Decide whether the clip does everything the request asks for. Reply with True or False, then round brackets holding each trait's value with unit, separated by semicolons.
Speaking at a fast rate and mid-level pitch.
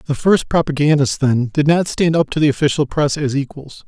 True (215 wpm; 145 Hz)